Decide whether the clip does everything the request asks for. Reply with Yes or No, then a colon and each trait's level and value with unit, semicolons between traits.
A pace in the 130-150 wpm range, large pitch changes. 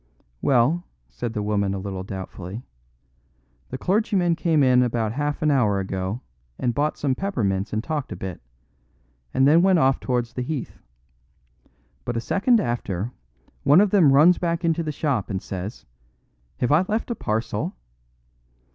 No: average, 160 wpm; wide, 7.4 semitones